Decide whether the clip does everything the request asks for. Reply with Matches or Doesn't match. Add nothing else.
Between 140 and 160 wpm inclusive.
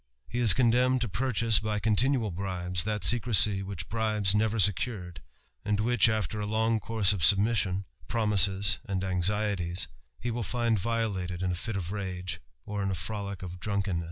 Doesn't match